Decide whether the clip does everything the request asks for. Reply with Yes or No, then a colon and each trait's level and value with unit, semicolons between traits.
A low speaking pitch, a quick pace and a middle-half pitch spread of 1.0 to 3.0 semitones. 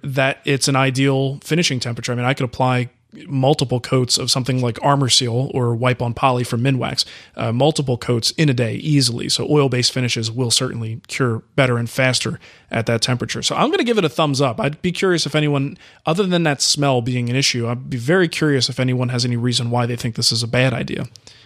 Yes: low, 130 Hz; fast, 230 wpm; average, 2.7 semitones